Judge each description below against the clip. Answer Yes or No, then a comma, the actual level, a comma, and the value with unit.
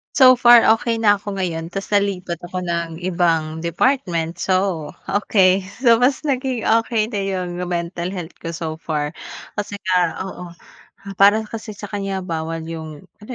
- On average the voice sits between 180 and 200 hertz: Yes, medium, 185 Hz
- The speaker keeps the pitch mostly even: No, average, 4.0 semitones